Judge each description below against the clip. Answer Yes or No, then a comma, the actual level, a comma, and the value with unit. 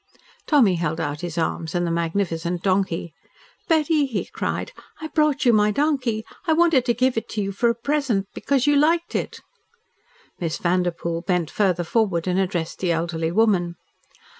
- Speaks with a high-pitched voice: Yes, high, 195 Hz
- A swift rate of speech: No, average, 170 wpm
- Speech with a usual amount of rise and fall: No, wide, 7.3 semitones